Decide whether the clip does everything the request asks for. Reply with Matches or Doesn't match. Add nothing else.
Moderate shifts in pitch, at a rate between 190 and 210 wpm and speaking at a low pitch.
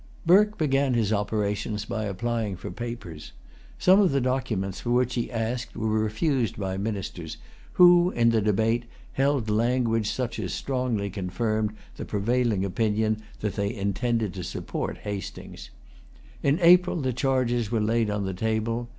Doesn't match